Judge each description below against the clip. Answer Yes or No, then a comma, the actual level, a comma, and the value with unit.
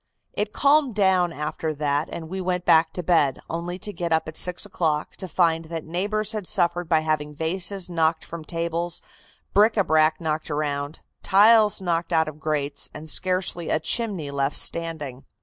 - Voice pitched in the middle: Yes, medium, 165 Hz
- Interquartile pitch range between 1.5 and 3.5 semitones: Yes, average, 2.9 semitones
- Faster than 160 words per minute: Yes, average, 180 wpm